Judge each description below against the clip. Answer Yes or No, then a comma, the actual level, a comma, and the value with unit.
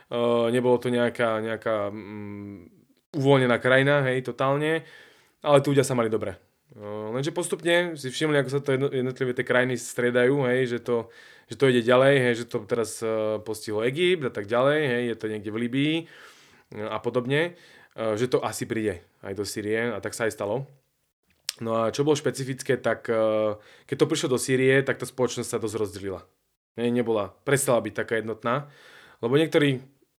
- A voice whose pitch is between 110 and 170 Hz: Yes, low, 125 Hz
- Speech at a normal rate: No, fast, 185 wpm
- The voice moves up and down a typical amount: Yes, average, 3.7 semitones